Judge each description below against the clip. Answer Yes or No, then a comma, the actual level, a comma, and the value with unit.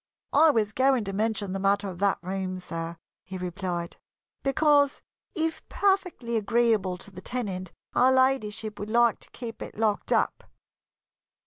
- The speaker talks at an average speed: Yes, average, 150 wpm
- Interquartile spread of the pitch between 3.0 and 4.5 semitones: No, average, 5.0 semitones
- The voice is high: Yes, high, 210 Hz